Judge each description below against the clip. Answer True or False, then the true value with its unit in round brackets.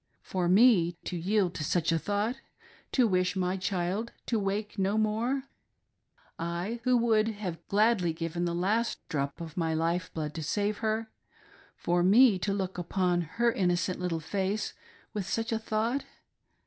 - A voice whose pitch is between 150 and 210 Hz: True (190 Hz)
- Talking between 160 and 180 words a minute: True (175 wpm)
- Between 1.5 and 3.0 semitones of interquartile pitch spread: False (3.8 semitones)